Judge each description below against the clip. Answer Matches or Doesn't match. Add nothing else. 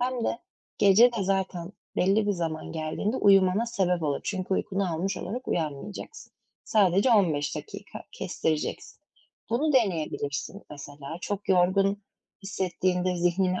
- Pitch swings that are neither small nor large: Matches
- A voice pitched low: Doesn't match